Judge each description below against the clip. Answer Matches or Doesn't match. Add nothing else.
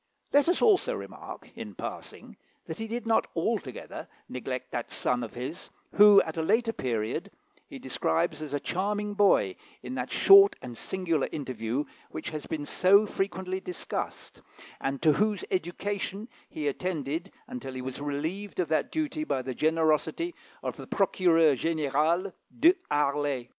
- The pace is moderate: Matches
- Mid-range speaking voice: Matches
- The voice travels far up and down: Matches